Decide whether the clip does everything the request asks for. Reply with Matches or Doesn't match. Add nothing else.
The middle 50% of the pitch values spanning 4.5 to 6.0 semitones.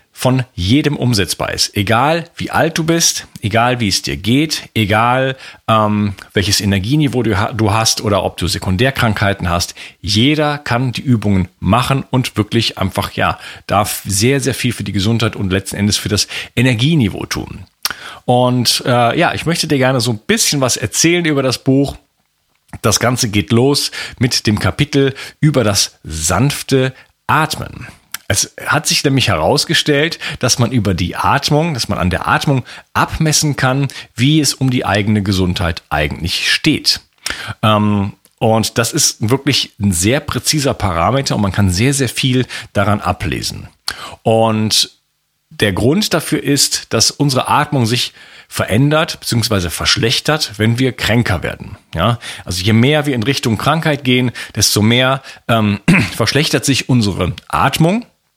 Matches